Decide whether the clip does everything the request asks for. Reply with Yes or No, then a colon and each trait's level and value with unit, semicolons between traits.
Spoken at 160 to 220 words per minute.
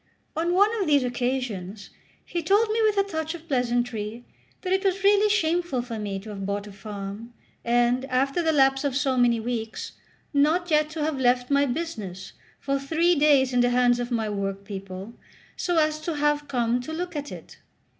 Yes: average, 195 wpm